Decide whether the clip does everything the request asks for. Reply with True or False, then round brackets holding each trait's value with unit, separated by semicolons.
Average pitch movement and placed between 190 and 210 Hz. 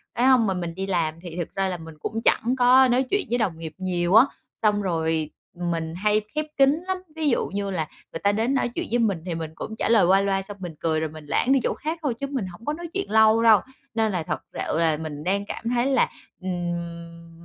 False (6.1 semitones; 195 Hz)